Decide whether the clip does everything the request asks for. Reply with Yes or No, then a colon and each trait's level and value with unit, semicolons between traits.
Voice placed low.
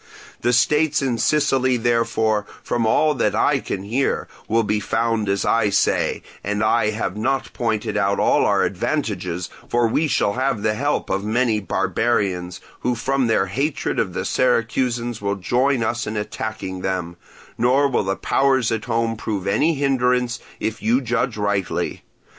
Yes: low, 115 Hz